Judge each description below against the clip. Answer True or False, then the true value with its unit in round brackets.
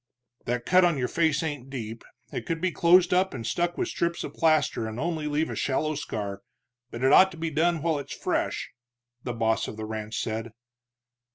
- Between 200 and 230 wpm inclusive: True (205 wpm)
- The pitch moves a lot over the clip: True (6.6 semitones)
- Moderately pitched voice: True (145 Hz)